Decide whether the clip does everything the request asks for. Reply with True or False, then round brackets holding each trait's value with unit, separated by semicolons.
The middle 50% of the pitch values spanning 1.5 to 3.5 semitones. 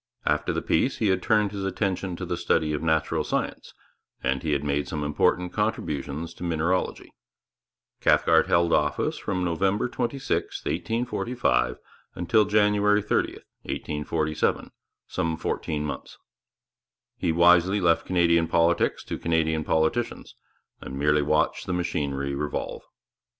False (4.2 semitones)